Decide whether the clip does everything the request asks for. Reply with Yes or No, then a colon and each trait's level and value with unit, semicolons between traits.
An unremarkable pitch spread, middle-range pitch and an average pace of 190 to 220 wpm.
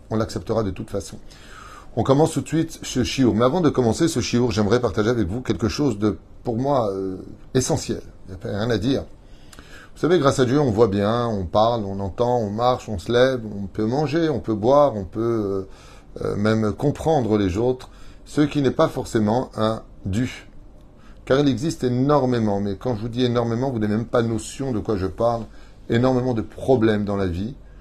No: average, 3.8 semitones; low, 115 Hz; average, 215 wpm